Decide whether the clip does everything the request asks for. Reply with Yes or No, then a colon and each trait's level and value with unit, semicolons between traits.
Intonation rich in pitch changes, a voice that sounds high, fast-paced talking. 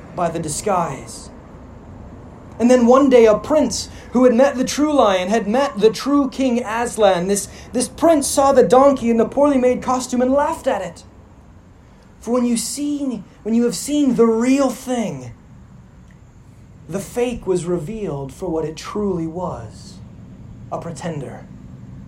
No: wide, 7.3 semitones; high, 230 Hz; average, 160 wpm